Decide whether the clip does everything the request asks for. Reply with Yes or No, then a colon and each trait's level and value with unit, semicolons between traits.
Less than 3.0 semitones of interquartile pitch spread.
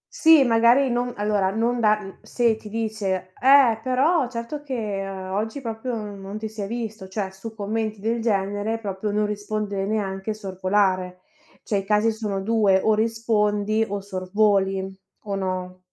Yes: narrow, 2.6 semitones